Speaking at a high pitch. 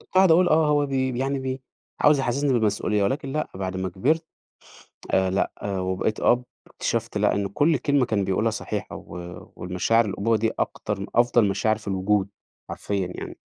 No: low, 115 Hz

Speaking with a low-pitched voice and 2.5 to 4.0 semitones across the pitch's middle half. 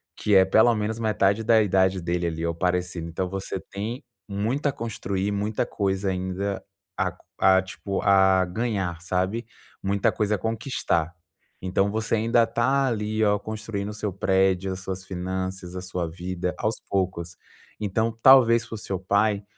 Yes: low, 100 Hz; average, 2.8 semitones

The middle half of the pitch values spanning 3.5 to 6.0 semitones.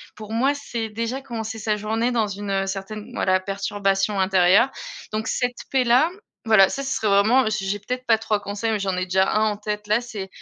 No: average, 2.7 semitones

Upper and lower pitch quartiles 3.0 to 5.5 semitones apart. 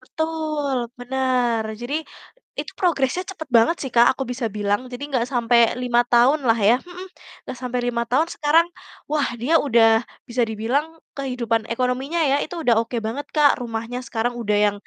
Yes: average, 3.6 semitones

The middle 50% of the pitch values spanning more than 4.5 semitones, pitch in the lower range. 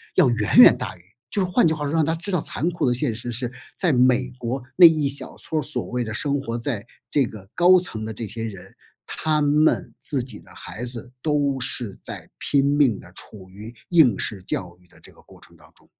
Yes: average, 5.2 semitones; low, 130 Hz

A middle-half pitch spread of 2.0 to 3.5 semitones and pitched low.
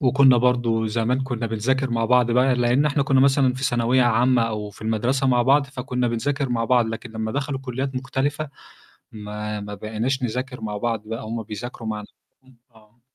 Yes: average, 2.8 semitones; low, 120 Hz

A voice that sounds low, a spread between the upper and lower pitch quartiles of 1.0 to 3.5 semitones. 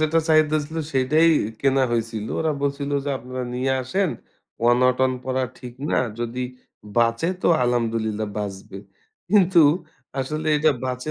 No: low, 130 Hz; average, 4.5 semitones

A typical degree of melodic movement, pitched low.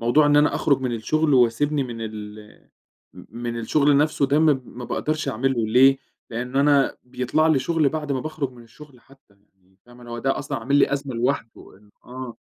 Yes: average, 3.6 semitones; low, 130 Hz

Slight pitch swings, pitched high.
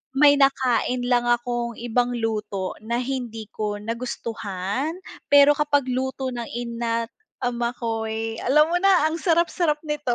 No: average, 3.6 semitones; high, 245 Hz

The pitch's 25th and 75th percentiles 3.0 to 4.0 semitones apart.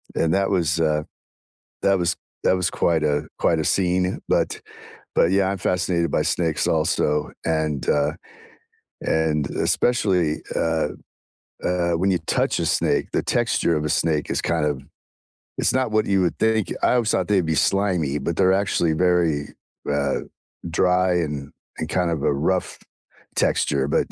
Yes: average, 3.3 semitones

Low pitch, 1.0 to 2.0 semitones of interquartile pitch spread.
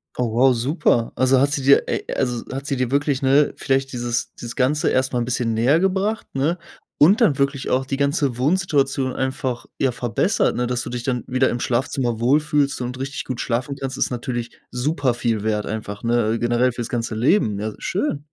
No: low, 130 Hz; average, 2.7 semitones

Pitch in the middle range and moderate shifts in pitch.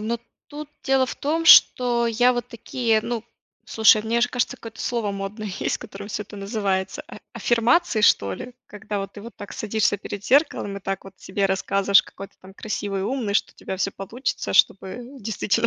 No: high, 215 Hz; average, 3.3 semitones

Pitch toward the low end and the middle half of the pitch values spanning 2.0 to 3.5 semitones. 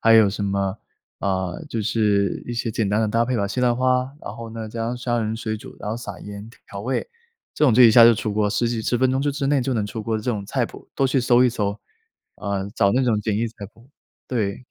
Yes: low, 115 Hz; average, 2.9 semitones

